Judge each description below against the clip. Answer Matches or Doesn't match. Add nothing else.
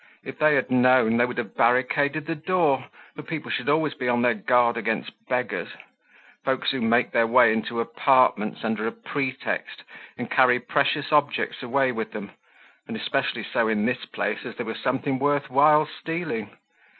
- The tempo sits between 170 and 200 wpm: Matches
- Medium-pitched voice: Doesn't match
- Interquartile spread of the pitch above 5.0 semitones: Doesn't match